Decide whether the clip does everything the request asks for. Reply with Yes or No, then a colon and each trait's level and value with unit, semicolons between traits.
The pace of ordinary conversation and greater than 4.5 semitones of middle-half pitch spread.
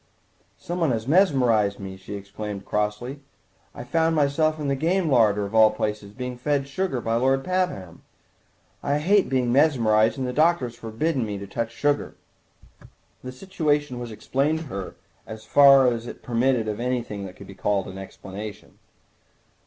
Yes: average, 170 wpm; wide, 5.4 semitones